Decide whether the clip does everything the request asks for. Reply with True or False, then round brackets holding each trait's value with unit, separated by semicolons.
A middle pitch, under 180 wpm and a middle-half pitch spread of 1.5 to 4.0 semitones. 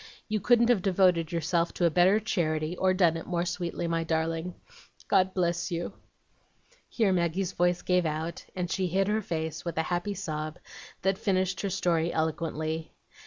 True (175 Hz; 170 wpm; 2.5 semitones)